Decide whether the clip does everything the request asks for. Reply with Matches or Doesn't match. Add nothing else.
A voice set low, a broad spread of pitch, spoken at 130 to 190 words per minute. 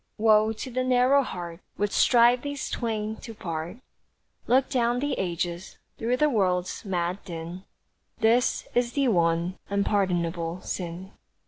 Doesn't match